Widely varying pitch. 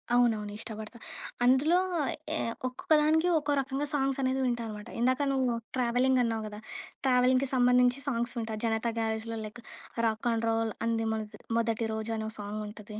No: average, 2.7 semitones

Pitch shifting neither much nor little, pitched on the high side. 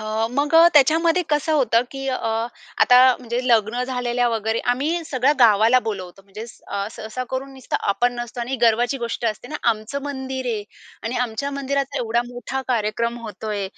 Yes: average, 3.2 semitones; high, 245 Hz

